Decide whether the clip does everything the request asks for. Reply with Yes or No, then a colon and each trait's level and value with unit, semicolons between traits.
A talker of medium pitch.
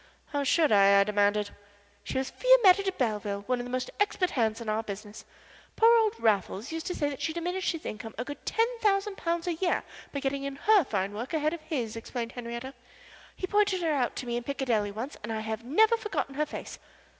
No: very high, 270 Hz